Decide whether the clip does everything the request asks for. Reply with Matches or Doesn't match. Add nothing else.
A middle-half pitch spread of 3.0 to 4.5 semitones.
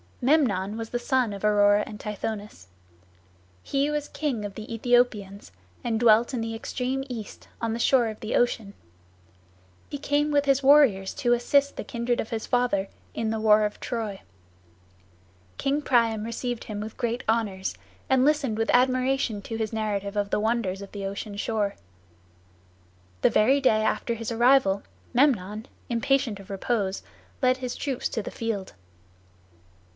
Matches